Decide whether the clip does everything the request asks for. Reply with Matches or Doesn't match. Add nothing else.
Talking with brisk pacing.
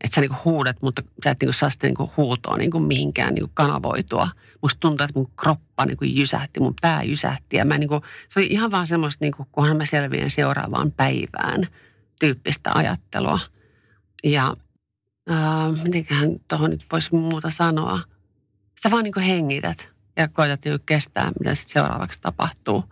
Matches